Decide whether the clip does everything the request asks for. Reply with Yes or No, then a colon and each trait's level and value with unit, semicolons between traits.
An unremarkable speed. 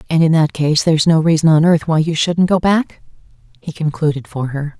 No: fast, 225 wpm